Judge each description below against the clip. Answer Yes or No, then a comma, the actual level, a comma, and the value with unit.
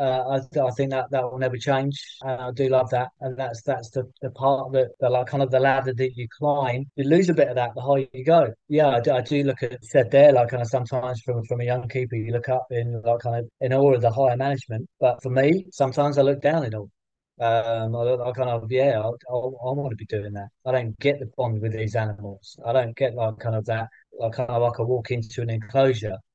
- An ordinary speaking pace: No, fast, 265 wpm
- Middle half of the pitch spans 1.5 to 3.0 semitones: Yes, narrow, 2.4 semitones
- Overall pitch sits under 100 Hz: No, low, 125 Hz